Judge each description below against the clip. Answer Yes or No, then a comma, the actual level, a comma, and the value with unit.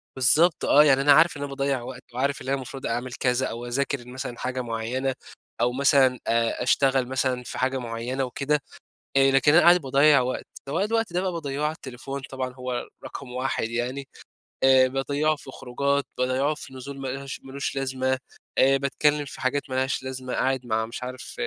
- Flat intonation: Yes, narrow, 1.7 semitones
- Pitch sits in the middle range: No, low, 130 Hz